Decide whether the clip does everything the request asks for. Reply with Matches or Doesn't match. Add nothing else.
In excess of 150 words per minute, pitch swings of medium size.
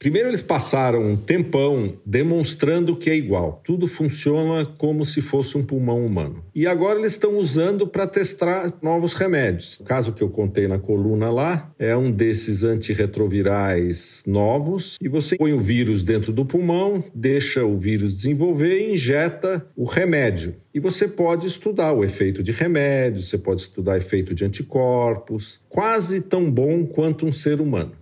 Doesn't match